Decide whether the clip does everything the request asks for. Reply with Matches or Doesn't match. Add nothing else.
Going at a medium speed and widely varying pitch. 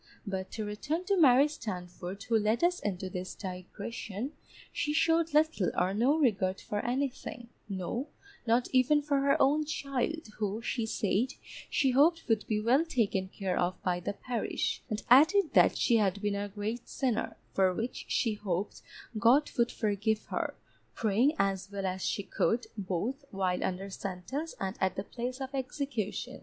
Matches